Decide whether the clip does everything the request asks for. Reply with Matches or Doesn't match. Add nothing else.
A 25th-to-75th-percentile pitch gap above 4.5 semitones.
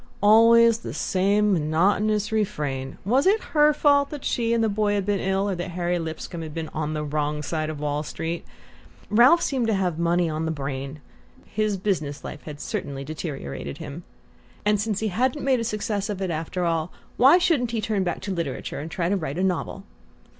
Matches